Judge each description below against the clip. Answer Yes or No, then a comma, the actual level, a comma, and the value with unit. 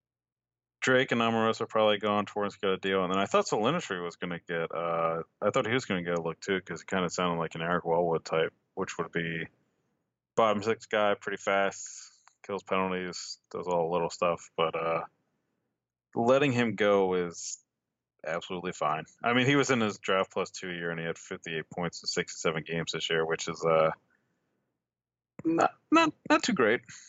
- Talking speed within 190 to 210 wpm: Yes, fast, 205 wpm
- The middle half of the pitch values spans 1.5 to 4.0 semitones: No, average, 5.0 semitones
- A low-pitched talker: Yes, very low, 95 Hz